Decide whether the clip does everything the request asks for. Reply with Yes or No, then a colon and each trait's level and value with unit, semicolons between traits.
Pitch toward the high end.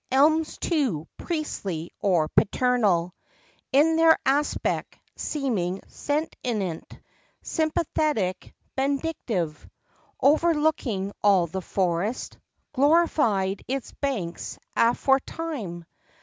Yes: very high, 250 Hz